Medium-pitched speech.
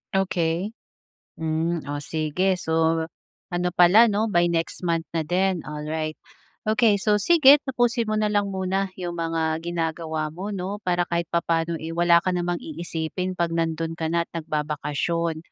Yes: medium, 170 Hz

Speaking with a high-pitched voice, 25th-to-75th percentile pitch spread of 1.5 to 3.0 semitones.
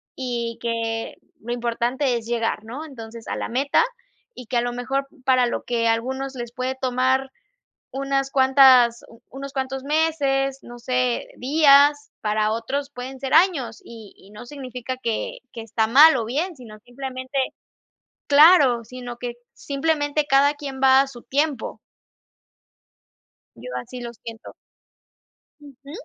Yes: very high, 260 Hz; average, 2.7 semitones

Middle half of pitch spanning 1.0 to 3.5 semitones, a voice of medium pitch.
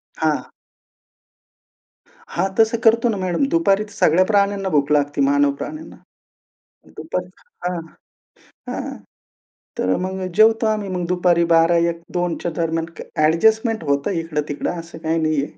No: average, 4.3 semitones; medium, 175 Hz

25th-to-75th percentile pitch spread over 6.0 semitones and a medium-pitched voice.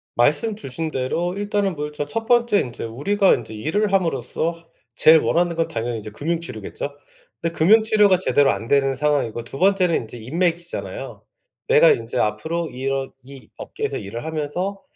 Yes: wide, 6.7 semitones; medium, 160 Hz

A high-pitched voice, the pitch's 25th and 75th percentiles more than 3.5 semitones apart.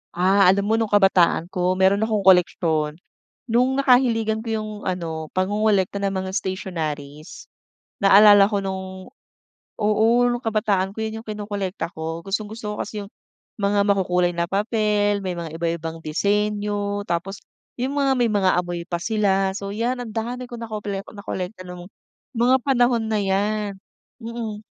No: high, 200 Hz; average, 2.9 semitones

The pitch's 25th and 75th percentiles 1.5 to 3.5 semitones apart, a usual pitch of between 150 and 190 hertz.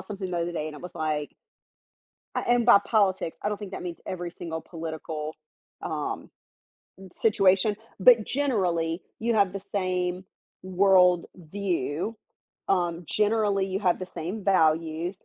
Yes: average, 3.1 semitones; medium, 185 Hz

